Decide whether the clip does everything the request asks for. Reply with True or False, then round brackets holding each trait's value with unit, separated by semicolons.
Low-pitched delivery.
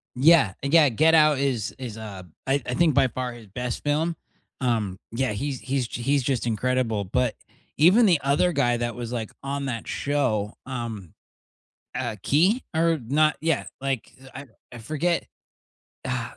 True (130 Hz)